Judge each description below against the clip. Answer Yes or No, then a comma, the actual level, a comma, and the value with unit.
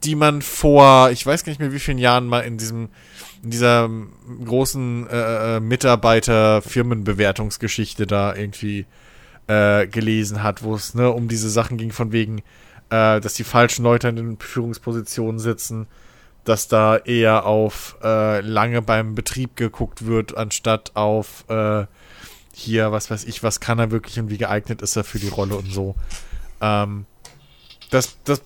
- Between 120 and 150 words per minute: No, average, 160 wpm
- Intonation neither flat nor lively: No, narrow, 2.1 semitones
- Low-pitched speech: Yes, low, 110 Hz